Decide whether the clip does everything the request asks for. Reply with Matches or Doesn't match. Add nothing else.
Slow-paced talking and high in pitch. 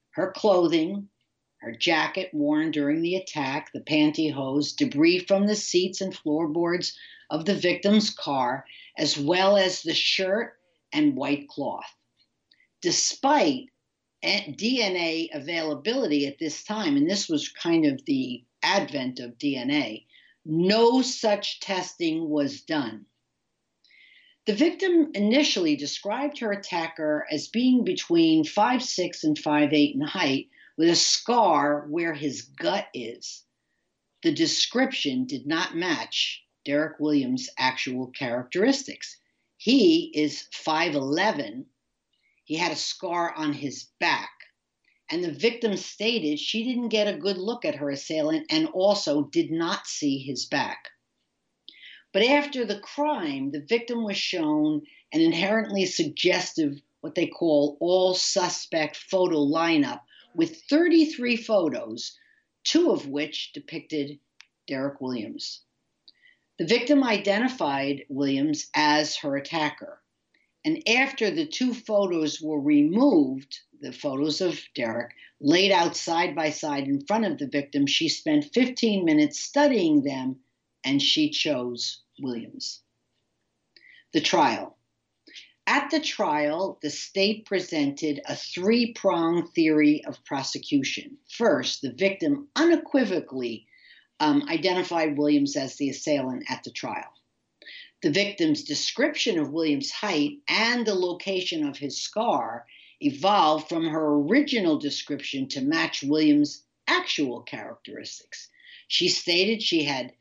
Matches